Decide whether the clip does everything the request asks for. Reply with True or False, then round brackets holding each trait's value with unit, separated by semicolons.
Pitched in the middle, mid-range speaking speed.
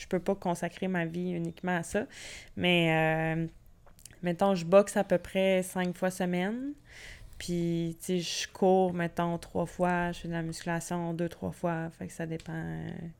True (175 Hz; 190 wpm)